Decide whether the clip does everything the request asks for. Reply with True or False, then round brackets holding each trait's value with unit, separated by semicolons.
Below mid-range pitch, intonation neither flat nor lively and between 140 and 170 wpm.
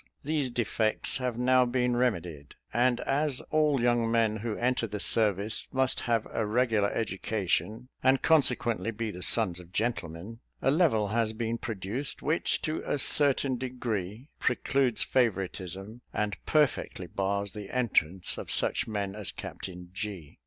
True (115 Hz; 3.9 semitones; 145 wpm)